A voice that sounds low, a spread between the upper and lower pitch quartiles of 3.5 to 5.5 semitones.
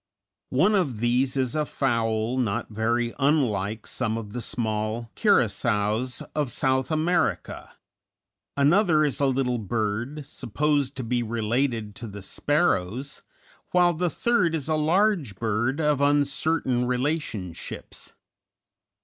Yes: low, 130 Hz; average, 5.0 semitones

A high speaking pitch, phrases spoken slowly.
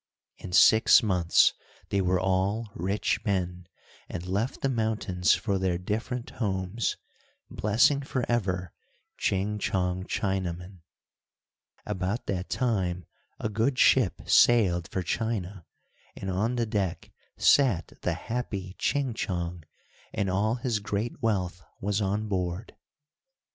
No: low, 100 Hz; slow, 120 wpm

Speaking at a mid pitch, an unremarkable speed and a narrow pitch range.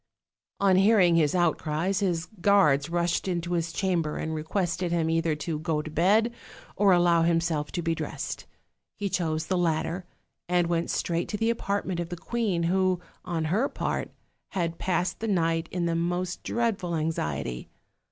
Yes: medium, 175 Hz; average, 165 wpm; narrow, 2.3 semitones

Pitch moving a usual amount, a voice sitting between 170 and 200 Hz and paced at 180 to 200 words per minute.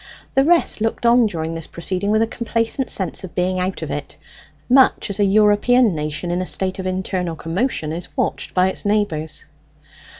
Yes: average, 4.2 semitones; high, 190 Hz; average, 190 wpm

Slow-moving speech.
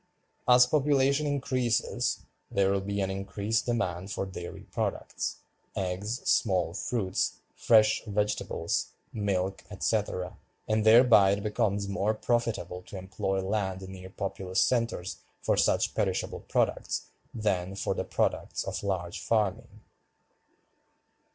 Yes: slow, 120 wpm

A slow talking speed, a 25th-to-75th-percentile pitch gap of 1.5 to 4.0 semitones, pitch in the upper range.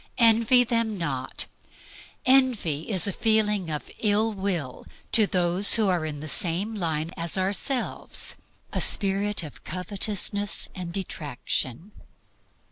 No: slow, 125 wpm; average, 4.4 semitones; high, 195 Hz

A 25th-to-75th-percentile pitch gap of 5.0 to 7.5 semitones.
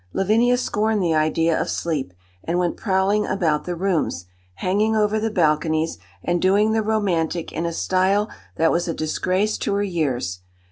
No: average, 4.2 semitones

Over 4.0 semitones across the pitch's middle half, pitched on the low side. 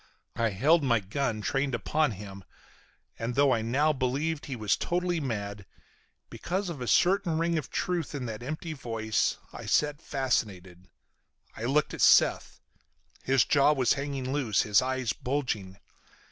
Yes: average, 5.2 semitones; low, 130 Hz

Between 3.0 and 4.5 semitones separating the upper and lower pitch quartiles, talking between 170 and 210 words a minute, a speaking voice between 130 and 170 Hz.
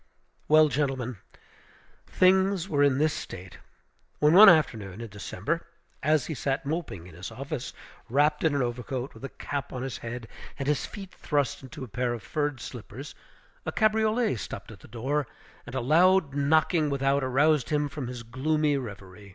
Yes: average, 4.2 semitones; average, 175 wpm; medium, 140 Hz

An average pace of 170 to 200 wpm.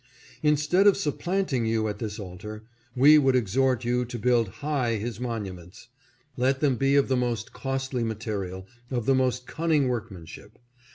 No: average, 160 wpm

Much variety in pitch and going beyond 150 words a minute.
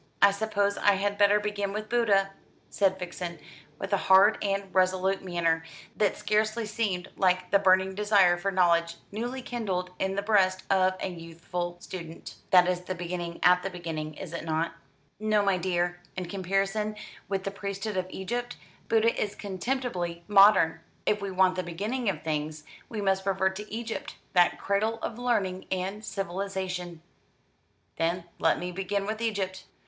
No: narrow, 2.4 semitones; average, 165 wpm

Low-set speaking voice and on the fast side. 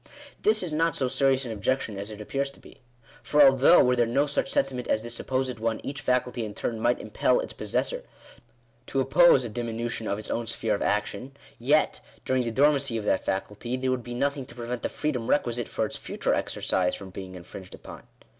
Yes: low, 125 Hz; fast, 220 wpm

